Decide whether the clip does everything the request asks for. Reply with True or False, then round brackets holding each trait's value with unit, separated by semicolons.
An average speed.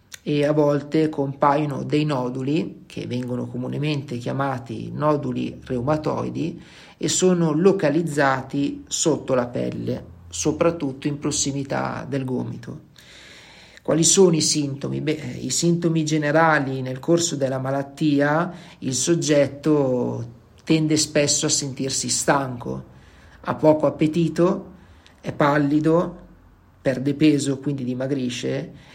False (105 wpm)